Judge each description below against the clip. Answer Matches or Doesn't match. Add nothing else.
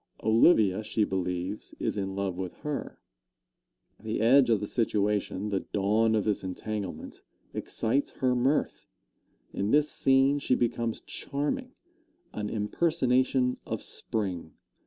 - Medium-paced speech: Doesn't match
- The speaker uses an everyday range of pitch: Matches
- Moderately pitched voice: Doesn't match